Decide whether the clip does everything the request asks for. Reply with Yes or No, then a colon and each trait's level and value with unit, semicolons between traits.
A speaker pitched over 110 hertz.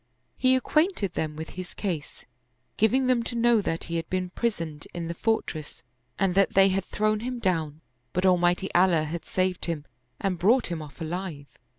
Yes: medium, 185 Hz